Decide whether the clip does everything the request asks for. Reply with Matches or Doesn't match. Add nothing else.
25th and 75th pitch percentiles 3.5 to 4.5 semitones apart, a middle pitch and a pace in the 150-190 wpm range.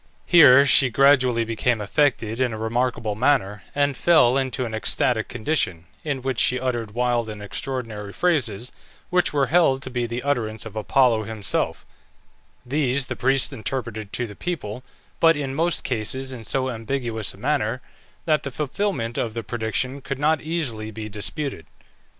Doesn't match